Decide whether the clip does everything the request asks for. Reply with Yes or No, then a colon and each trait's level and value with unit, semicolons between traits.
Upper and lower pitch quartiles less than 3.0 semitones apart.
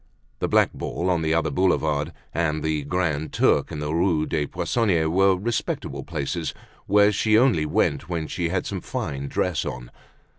No: average, 3.3 semitones